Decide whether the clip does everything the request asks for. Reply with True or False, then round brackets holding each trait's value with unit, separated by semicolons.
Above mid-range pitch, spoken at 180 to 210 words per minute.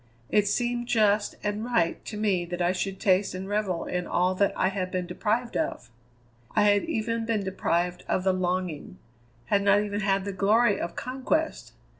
True (200 Hz; 185 wpm)